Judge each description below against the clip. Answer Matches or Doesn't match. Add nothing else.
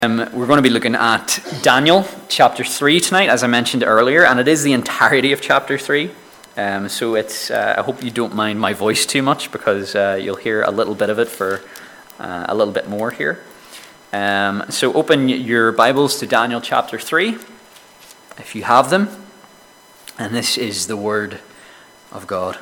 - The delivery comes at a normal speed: Matches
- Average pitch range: Matches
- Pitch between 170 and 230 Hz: Doesn't match